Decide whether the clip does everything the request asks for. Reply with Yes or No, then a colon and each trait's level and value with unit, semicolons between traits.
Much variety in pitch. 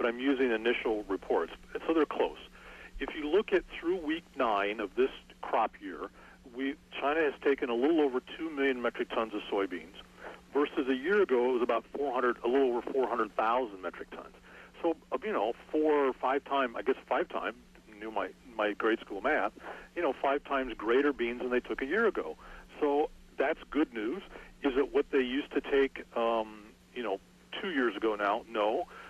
Yes: wide, 5.7 semitones